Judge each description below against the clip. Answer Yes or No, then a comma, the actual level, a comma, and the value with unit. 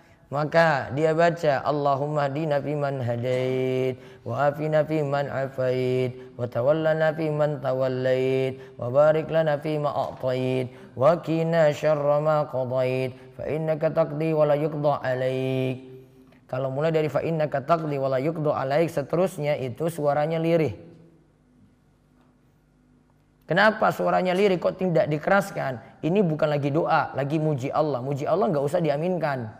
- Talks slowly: No, average, 130 wpm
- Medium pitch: Yes, medium, 145 Hz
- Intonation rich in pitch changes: No, average, 3.4 semitones